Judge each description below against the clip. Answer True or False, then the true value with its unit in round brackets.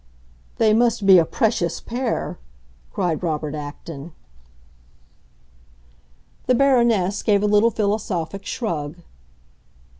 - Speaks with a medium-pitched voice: False (200 Hz)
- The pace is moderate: False (95 wpm)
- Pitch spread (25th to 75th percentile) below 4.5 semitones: False (5.3 semitones)